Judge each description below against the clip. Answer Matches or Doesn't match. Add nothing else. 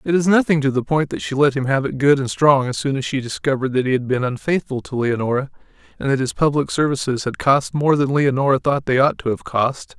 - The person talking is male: Matches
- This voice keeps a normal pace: Doesn't match